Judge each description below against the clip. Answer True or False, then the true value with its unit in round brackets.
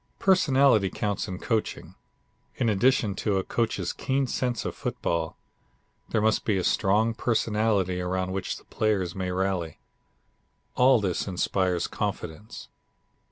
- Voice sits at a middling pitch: False (100 Hz)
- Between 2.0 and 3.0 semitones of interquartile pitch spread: False (3.6 semitones)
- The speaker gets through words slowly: True (130 wpm)